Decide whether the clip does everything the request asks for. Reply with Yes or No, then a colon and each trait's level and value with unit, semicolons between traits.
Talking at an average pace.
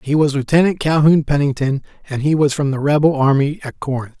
No: fast, 215 wpm